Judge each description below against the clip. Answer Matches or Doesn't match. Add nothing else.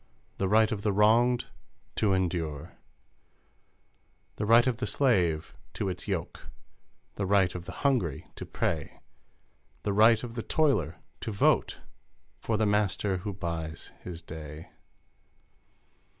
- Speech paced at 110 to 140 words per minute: Matches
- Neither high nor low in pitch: Doesn't match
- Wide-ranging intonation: Doesn't match